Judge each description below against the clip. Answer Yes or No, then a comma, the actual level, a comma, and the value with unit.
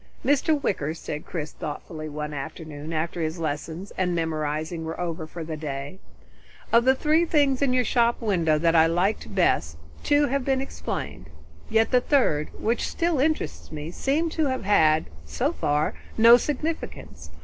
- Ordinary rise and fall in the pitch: No, wide, 8.8 semitones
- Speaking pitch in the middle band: Yes, medium, 170 Hz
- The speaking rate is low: No, average, 165 wpm